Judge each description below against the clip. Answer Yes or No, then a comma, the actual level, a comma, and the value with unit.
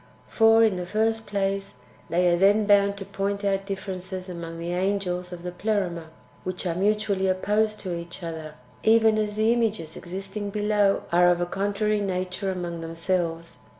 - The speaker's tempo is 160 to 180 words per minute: Yes, average, 170 wpm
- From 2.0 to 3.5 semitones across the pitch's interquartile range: Yes, average, 2.8 semitones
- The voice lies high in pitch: Yes, high, 195 Hz